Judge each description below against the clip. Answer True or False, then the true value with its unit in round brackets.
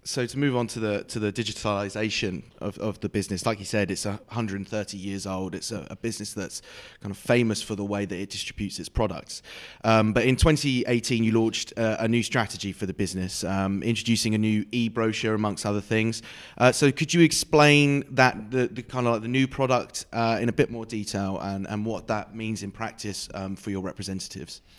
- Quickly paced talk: True (215 wpm)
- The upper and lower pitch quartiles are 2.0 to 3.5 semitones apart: True (2.9 semitones)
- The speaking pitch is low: True (110 Hz)